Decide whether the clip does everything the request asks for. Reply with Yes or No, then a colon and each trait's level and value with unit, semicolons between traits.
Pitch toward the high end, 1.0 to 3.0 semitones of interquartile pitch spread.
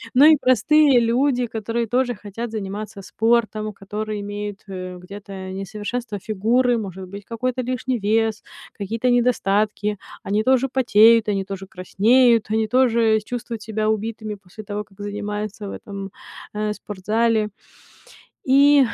Yes: high, 215 Hz; narrow, 2.6 semitones